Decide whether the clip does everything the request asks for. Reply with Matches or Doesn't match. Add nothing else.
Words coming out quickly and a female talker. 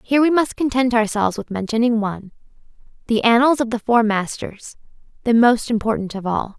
Doesn't match